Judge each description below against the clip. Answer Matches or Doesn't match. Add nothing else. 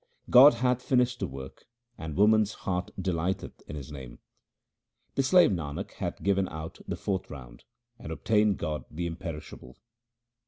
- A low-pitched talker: Matches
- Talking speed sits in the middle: Matches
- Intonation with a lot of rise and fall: Matches